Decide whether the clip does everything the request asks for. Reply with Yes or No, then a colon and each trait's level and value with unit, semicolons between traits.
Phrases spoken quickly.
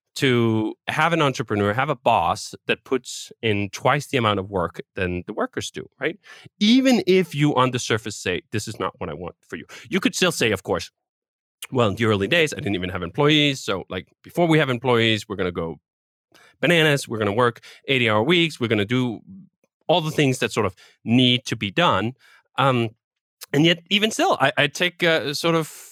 Yes: fast, 220 wpm